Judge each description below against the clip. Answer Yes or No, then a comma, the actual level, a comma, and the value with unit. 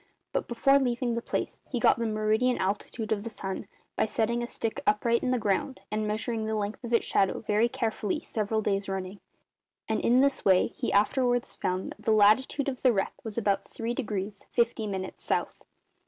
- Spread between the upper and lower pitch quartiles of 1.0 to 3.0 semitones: Yes, narrow, 2.6 semitones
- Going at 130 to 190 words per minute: No, average, 200 wpm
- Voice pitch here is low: No, high, 220 Hz